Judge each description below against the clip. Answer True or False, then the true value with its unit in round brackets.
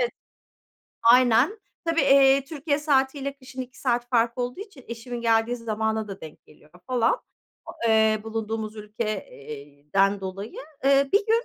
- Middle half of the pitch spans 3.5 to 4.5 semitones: True (4.0 semitones)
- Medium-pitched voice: False (235 Hz)